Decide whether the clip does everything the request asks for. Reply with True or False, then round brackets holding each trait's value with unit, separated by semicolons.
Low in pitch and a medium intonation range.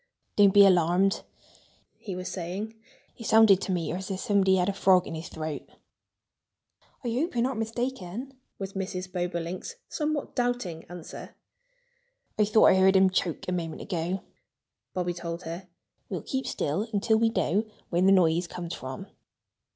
False (190 Hz; 3.6 semitones)